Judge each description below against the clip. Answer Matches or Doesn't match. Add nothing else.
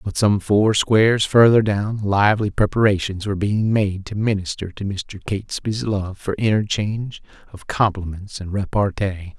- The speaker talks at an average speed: Matches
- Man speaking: Matches